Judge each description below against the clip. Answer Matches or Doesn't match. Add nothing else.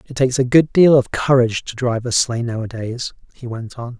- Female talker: Doesn't match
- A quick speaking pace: Matches